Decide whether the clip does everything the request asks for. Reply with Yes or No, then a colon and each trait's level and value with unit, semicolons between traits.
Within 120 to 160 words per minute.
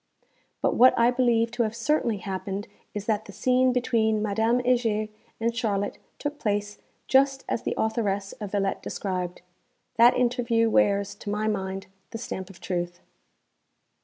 Yes: average, 155 wpm